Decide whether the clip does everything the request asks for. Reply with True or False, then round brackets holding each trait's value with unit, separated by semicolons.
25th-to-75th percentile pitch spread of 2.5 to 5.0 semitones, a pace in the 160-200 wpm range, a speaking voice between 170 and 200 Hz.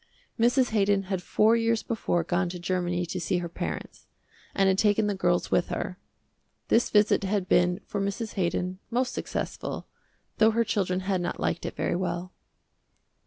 True (3.2 semitones; 170 wpm; 190 Hz)